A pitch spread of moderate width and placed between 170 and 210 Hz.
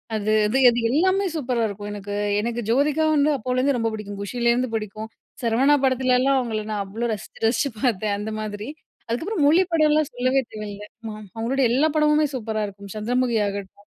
No: average, 4.2 semitones; high, 235 Hz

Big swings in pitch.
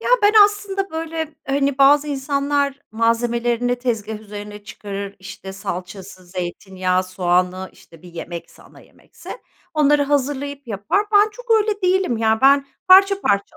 Yes: wide, 7.1 semitones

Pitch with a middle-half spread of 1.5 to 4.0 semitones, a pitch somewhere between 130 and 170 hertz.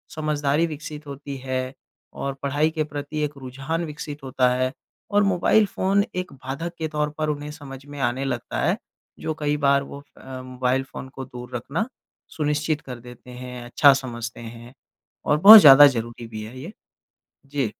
Yes: average, 2.9 semitones; medium, 140 Hz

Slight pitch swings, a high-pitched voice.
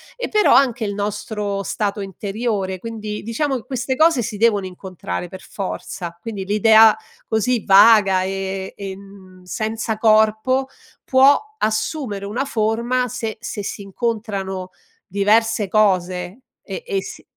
No: average, 3.0 semitones; high, 215 Hz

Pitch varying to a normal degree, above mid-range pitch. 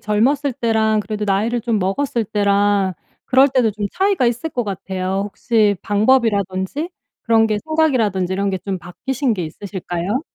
Yes: average, 3.9 semitones; high, 215 Hz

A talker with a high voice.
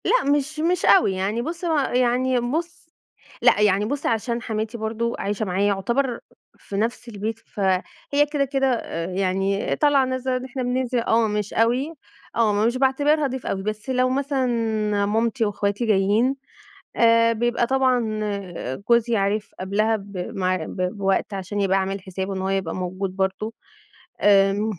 Yes: high, 225 Hz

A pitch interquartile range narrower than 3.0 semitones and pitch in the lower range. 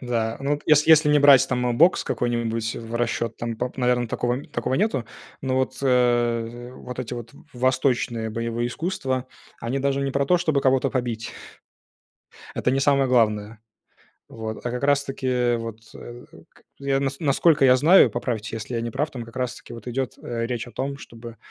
Yes: narrow, 2.6 semitones; low, 125 Hz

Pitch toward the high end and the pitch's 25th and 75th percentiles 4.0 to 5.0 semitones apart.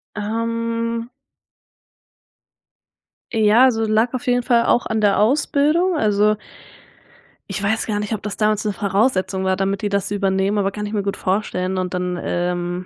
No: high, 210 Hz; average, 2.9 semitones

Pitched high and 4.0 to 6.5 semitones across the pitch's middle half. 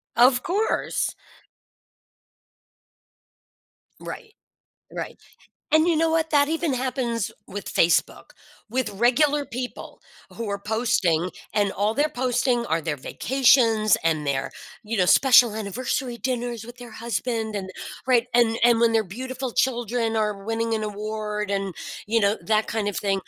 No: high, 230 Hz; average, 3.5 semitones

